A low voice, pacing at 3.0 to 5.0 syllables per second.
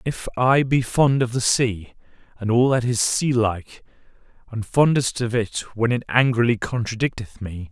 Yes: low, 120 Hz; 4.8 syllables/s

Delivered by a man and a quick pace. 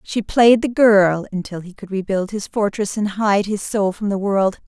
No: female; fast, 220 wpm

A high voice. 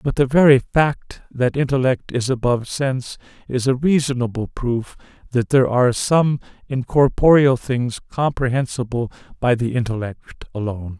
No: low, 125 Hz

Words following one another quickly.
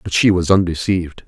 No: average, 190 wpm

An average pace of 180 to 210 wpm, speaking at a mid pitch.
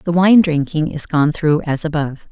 Yes: fast, 205 wpm; medium, 160 Hz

